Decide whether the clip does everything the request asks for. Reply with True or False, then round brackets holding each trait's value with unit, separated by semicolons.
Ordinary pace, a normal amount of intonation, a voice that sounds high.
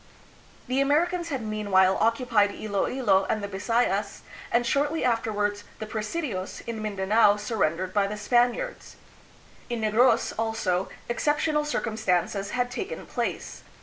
False (130 wpm; 3.6 semitones; 220 Hz)